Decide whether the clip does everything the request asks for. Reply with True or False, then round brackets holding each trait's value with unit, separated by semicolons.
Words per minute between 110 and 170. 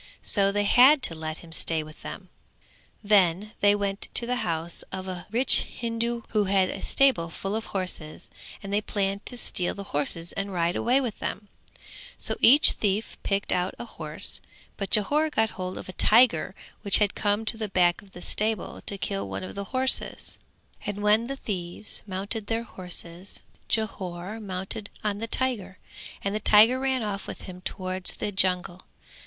False (180 wpm)